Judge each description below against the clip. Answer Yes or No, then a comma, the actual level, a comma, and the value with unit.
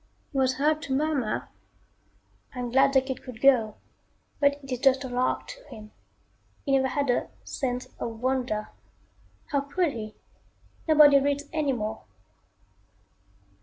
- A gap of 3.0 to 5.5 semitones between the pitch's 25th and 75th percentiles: No, narrow, 2.4 semitones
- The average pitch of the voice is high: Yes, very high, 265 Hz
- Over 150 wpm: No, average, 145 wpm